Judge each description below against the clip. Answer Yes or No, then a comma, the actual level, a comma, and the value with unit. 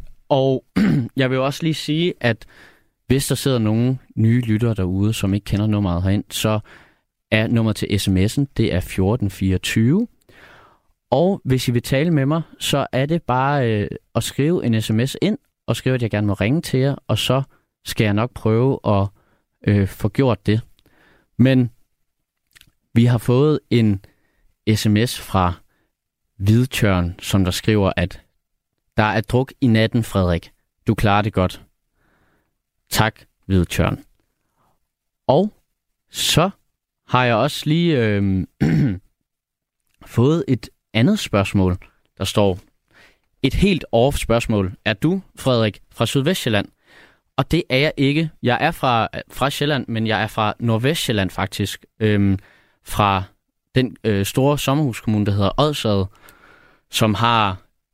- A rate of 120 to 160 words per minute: Yes, slow, 145 wpm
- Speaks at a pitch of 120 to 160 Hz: No, low, 110 Hz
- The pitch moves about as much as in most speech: Yes, average, 4.7 semitones